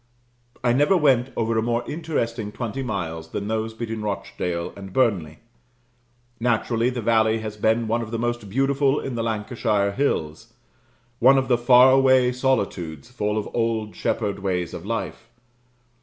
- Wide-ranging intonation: No, average, 3.1 semitones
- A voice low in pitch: Yes, low, 115 Hz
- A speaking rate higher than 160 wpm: No, average, 155 wpm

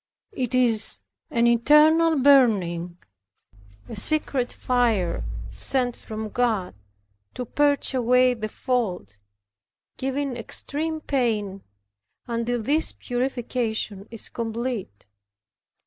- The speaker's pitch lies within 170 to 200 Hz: No, high, 245 Hz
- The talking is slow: Yes, slow, 90 wpm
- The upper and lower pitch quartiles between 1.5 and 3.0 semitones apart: No, average, 3.4 semitones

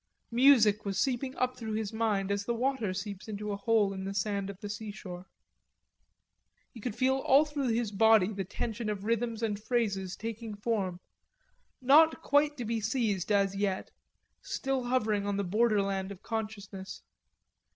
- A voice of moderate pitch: No, high, 215 Hz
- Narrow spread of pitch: No, average, 3.1 semitones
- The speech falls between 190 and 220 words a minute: No, average, 170 wpm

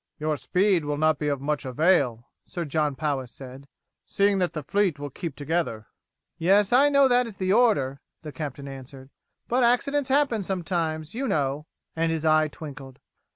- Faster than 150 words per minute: Yes, average, 175 wpm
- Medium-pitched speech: Yes, medium, 155 Hz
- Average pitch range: No, wide, 5.9 semitones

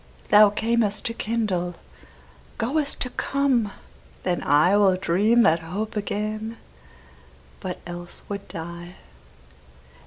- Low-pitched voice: No, high, 205 Hz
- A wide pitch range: No, average, 4.3 semitones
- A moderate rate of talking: No, slow, 100 wpm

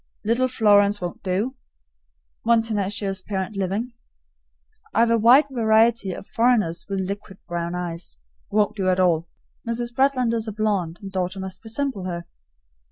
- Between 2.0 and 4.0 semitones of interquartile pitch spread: Yes, average, 3.7 semitones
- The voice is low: No, high, 205 Hz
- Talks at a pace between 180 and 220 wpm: No, average, 150 wpm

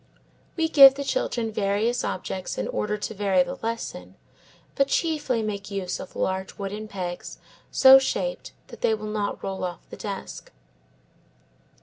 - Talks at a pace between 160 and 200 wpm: No, average, 150 wpm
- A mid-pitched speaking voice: No, high, 210 Hz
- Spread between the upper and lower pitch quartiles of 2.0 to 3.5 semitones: No, average, 5.2 semitones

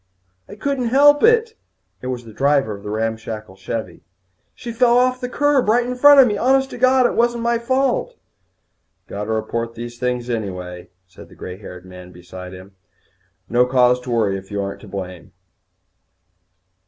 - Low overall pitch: Yes, low, 125 Hz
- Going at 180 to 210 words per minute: Yes, average, 185 wpm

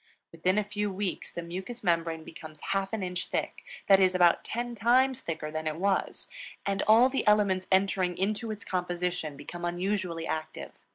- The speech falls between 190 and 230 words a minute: No, average, 175 wpm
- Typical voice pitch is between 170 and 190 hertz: Yes, medium, 185 Hz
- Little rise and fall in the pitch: No, average, 3.3 semitones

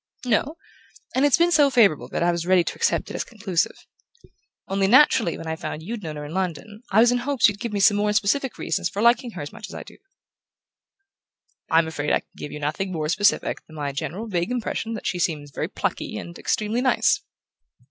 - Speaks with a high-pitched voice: Yes, high, 200 Hz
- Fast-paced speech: Yes, fast, 220 wpm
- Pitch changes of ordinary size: No, wide, 6.2 semitones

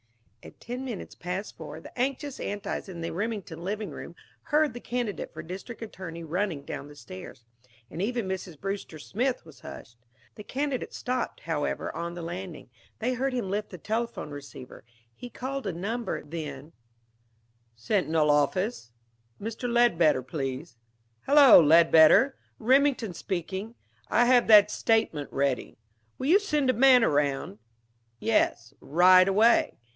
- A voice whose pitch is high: Yes, high, 195 Hz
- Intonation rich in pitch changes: Yes, wide, 7.0 semitones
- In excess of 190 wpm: No, average, 145 wpm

